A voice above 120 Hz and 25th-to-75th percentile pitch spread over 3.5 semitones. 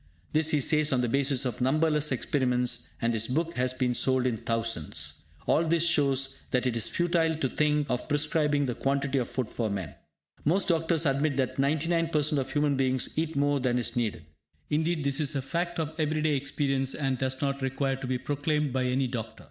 No: medium, 140 Hz; average, 3.2 semitones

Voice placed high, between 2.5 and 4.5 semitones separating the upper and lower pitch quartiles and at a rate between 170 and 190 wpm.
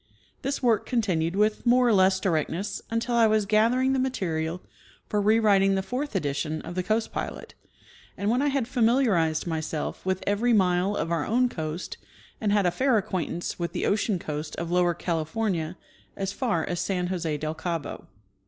No: high, 195 Hz; average, 5.1 semitones; average, 185 wpm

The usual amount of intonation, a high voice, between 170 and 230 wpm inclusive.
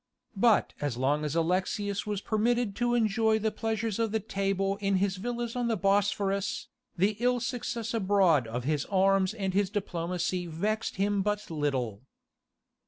No: average, 3.3 semitones; high, 200 Hz; average, 160 wpm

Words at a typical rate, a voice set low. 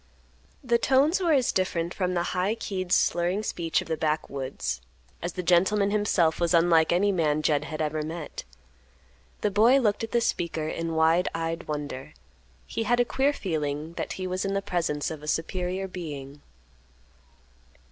No: average, 170 wpm; medium, 175 Hz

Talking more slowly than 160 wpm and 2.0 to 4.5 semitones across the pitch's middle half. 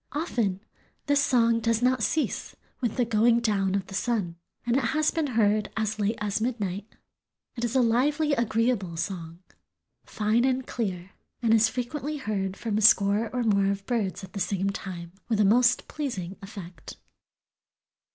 No: average, 170 wpm; average, 3.7 semitones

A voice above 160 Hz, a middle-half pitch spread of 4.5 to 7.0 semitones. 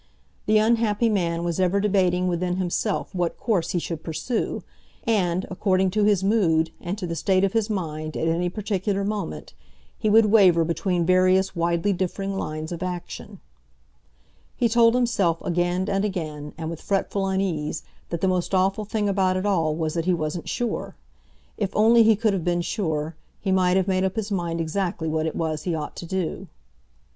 No: medium, 185 Hz; average, 3.2 semitones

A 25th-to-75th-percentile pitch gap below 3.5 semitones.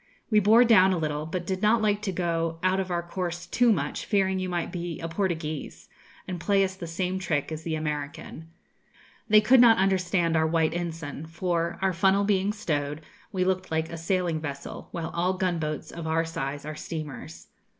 Yes: average, 2.9 semitones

